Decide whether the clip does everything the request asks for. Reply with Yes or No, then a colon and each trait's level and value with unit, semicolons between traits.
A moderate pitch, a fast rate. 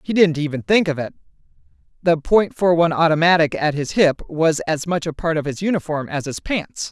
Yes: medium, 160 Hz; fast, 215 wpm